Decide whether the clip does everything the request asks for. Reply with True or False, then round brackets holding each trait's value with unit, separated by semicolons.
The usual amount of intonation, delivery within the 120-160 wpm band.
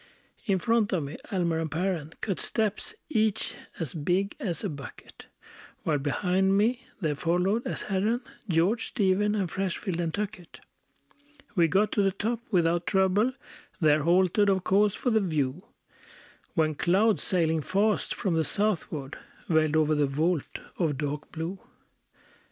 True (4.2 semitones; 150 wpm)